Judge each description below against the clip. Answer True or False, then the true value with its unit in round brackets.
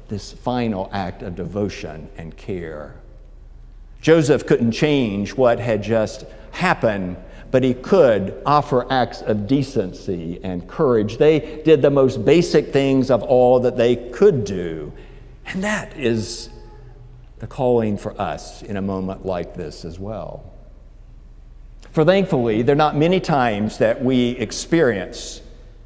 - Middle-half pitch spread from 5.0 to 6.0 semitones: True (5.6 semitones)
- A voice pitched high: False (115 Hz)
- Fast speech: False (135 wpm)